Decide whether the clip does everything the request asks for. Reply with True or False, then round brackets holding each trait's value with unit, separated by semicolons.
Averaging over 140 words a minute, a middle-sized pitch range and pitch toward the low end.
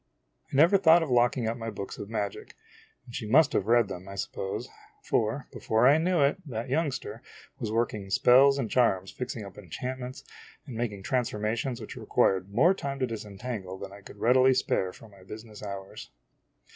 True (190 wpm; 4.3 semitones; 115 Hz)